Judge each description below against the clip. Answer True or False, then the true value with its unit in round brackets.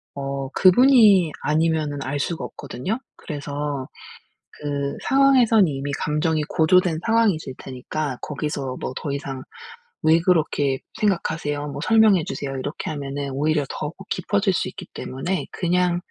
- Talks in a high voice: False (150 Hz)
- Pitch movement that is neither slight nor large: True (4.3 semitones)